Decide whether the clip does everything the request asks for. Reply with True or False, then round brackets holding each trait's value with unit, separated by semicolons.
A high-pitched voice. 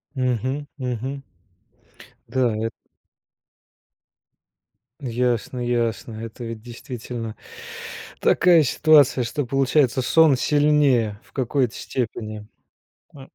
False (125 Hz)